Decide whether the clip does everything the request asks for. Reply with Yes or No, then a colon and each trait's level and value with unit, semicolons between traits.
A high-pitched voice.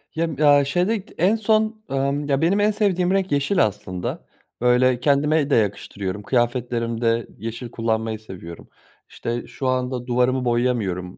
No: low, 125 Hz